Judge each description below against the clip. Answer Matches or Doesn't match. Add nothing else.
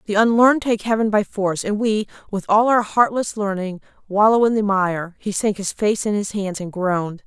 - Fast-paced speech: Matches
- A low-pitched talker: Doesn't match